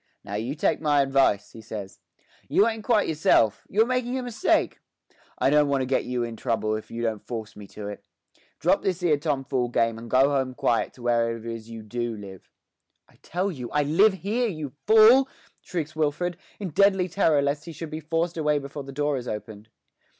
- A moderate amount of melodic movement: No, wide, 6.8 semitones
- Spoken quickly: Yes, fast, 210 wpm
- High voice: No, medium, 140 Hz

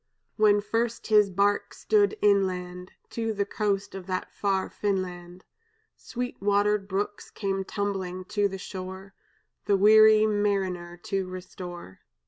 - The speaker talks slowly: Yes, slow, 125 wpm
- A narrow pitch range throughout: Yes, narrow, 2.0 semitones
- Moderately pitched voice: No, high, 195 Hz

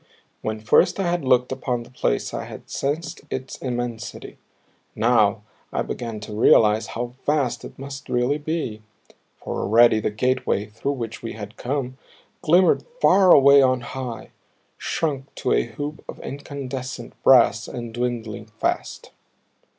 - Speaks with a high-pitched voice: No, low, 125 Hz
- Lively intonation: No, average, 3.5 semitones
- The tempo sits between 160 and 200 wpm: No, average, 145 wpm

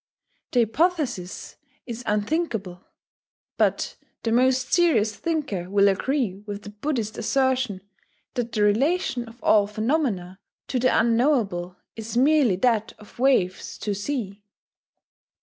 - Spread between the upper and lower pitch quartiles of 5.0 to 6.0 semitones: No, average, 4.4 semitones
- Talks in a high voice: Yes, high, 230 Hz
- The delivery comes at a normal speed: No, slow, 120 wpm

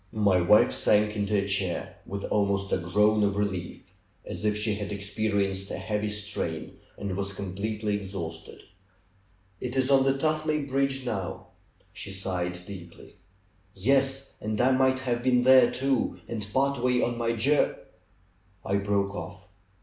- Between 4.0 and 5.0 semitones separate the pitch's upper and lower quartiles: Yes, average, 4.3 semitones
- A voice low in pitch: Yes, low, 105 Hz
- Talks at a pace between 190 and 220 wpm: No, average, 155 wpm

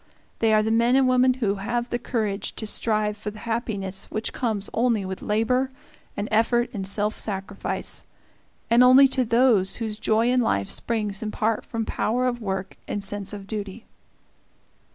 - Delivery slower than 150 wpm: No, average, 175 wpm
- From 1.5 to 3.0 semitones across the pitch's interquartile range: Yes, average, 2.7 semitones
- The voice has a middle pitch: No, high, 220 Hz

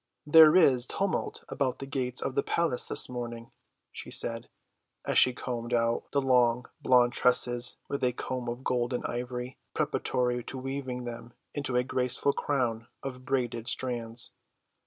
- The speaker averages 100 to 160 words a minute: Yes, average, 155 wpm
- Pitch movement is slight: Yes, narrow, 1.6 semitones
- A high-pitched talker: No, low, 125 Hz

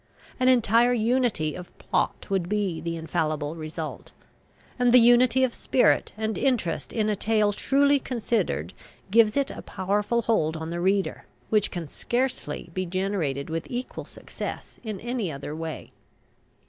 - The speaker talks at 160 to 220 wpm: No, average, 150 wpm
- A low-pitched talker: No, high, 205 Hz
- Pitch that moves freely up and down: Yes, wide, 6.4 semitones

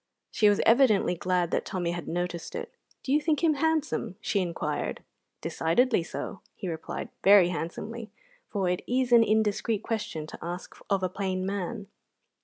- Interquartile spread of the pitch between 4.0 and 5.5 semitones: Yes, average, 4.5 semitones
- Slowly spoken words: No, average, 165 wpm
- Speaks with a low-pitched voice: No, high, 200 Hz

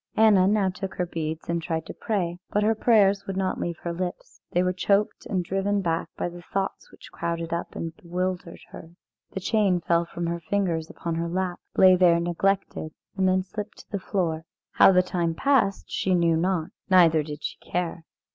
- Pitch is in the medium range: Yes, medium, 180 Hz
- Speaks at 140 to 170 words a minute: No, average, 200 wpm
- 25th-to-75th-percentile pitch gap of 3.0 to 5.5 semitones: No, narrow, 2.4 semitones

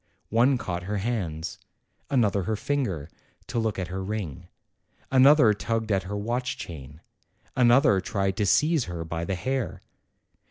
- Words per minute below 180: Yes, average, 150 wpm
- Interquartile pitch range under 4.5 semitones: No, average, 4.9 semitones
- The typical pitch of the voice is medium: No, low, 105 Hz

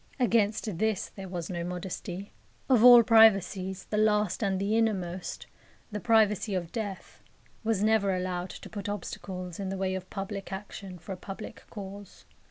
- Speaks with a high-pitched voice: Yes, high, 195 Hz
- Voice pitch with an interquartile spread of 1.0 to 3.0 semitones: Yes, narrow, 2.5 semitones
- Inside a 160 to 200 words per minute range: Yes, average, 165 wpm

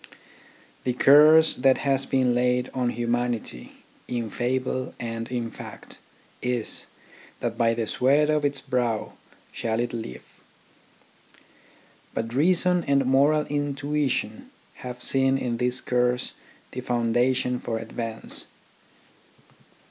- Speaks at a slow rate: Yes, slow, 120 wpm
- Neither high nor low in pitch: No, low, 125 Hz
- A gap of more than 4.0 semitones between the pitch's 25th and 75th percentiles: No, narrow, 2.4 semitones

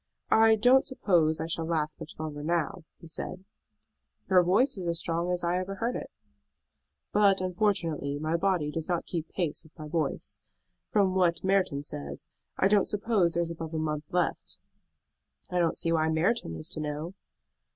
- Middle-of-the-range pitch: Yes, medium, 170 Hz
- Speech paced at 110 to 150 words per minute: No, average, 180 wpm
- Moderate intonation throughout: Yes, average, 3.2 semitones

